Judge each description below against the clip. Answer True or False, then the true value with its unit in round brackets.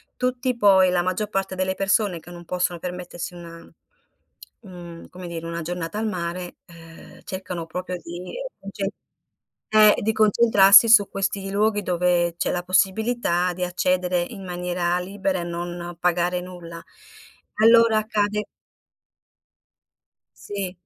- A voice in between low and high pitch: True (180 Hz)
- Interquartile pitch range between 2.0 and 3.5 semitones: True (2.6 semitones)